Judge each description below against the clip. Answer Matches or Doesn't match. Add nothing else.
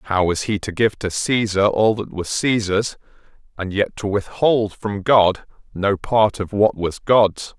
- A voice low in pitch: Matches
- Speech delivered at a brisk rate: Doesn't match